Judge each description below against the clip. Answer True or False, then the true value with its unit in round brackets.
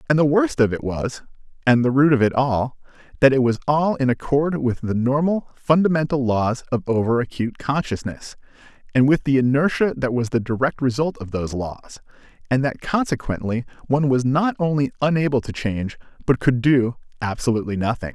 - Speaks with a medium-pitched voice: False (130 Hz)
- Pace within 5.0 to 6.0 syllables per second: True (5.5 syllables/s)